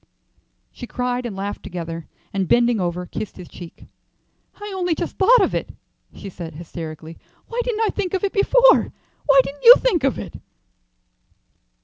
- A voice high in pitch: Yes, high, 245 Hz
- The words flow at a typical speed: Yes, average, 165 wpm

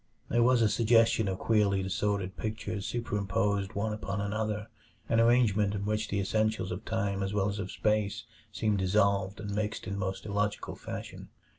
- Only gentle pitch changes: Yes, narrow, 1.7 semitones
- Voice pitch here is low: Yes, low, 105 Hz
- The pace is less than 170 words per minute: No, average, 175 wpm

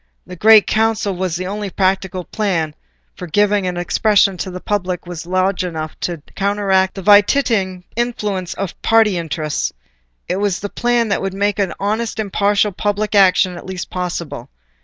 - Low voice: No, high, 195 Hz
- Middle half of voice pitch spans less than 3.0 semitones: Yes, narrow, 2.4 semitones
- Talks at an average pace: Yes, average, 160 wpm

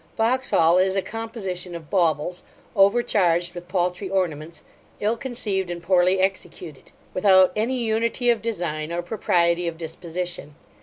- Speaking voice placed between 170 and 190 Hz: Yes, medium, 185 Hz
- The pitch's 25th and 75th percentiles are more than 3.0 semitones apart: Yes, average, 3.7 semitones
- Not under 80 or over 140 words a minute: Yes, slow, 135 wpm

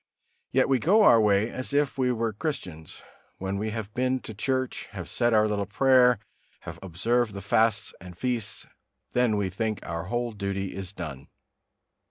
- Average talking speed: Yes, average, 175 wpm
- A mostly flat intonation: No, average, 4.2 semitones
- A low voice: Yes, low, 110 Hz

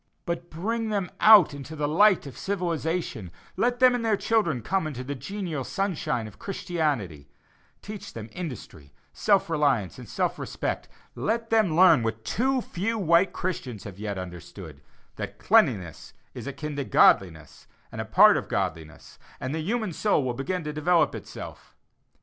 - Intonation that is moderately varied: No, wide, 8.0 semitones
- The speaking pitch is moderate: Yes, medium, 160 Hz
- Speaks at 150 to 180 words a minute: Yes, average, 160 wpm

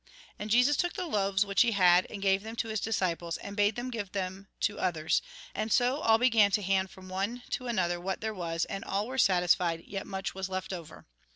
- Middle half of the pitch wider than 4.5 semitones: No, average, 3.1 semitones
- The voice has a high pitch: Yes, high, 195 Hz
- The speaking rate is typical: No, fast, 225 wpm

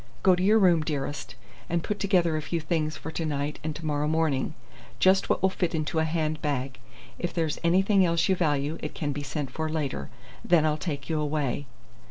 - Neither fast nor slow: No, fast, 215 wpm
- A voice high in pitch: No, medium, 155 Hz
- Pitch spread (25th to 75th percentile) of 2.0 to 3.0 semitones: Yes, narrow, 2.6 semitones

